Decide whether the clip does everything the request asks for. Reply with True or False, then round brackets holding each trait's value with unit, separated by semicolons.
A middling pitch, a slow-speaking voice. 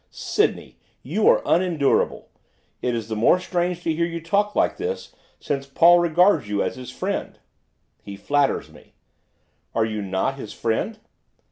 False (155 Hz; 155 wpm)